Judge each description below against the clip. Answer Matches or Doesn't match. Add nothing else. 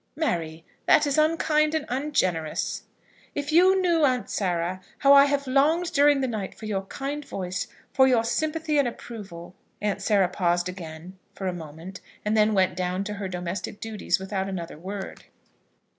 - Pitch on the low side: Doesn't match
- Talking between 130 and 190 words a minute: Matches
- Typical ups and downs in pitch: Doesn't match